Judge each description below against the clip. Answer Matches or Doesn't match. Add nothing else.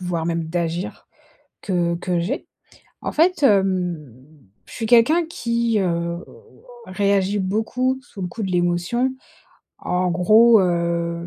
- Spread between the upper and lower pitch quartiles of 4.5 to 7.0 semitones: Matches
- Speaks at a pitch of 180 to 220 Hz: Matches